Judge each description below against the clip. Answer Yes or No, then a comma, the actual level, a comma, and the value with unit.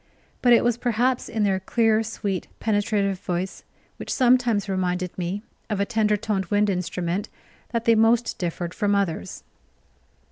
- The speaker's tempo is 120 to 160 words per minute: Yes, average, 150 wpm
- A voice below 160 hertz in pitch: No, high, 205 Hz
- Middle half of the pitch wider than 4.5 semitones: No, average, 3.3 semitones